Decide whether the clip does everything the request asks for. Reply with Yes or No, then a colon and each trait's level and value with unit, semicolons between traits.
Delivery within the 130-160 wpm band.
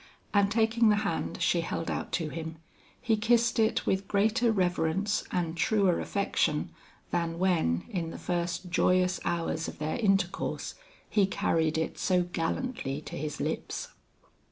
Yes: average, 150 wpm